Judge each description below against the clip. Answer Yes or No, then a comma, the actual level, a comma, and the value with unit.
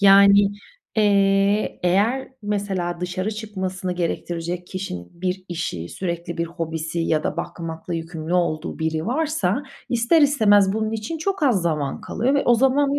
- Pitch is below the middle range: No, high, 190 Hz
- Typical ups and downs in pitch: Yes, average, 4.1 semitones